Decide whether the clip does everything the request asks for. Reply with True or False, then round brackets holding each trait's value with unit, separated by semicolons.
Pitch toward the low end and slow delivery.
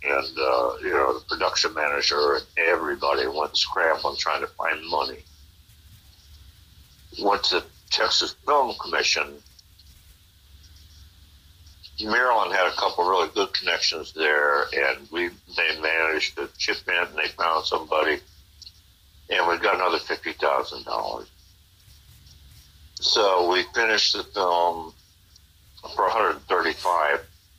True (85 Hz; 125 wpm)